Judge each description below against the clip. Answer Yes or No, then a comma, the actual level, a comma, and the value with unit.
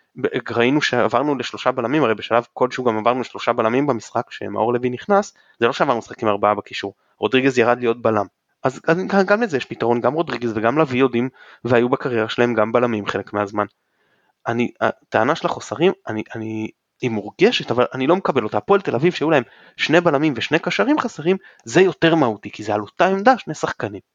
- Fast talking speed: Yes, fast, 185 wpm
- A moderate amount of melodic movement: No, wide, 6.2 semitones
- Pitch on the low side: Yes, low, 125 Hz